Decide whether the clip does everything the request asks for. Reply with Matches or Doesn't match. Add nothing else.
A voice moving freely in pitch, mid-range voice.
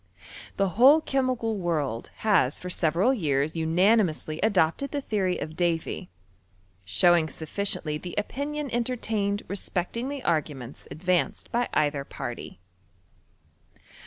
Matches